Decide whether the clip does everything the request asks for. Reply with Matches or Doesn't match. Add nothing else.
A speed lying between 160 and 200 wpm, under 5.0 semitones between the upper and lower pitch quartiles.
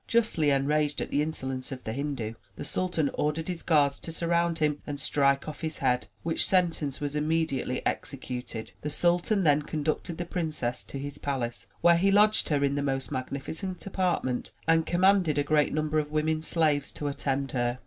Matches